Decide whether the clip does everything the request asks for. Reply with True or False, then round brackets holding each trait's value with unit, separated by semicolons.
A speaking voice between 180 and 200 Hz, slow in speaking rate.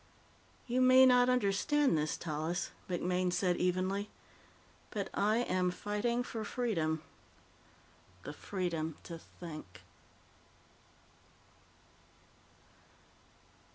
True (185 Hz; 85 wpm)